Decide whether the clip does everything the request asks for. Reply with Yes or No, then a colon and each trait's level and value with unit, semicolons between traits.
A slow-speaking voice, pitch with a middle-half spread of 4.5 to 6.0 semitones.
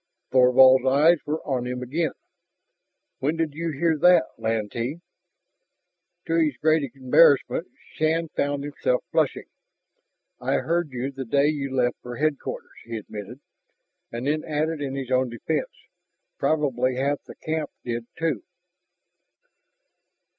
No: slow, 130 wpm; average, 3.7 semitones